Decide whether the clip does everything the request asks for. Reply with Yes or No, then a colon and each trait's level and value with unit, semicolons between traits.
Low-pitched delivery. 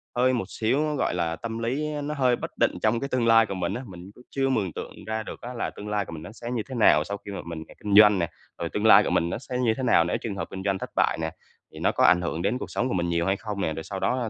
Yes: low, 105 Hz